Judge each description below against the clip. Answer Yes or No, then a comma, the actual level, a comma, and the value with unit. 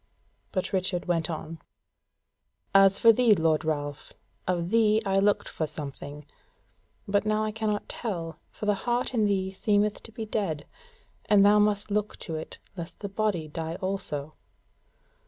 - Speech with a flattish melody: No, average, 4.3 semitones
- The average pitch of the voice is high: Yes, high, 195 Hz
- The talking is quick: No, average, 155 wpm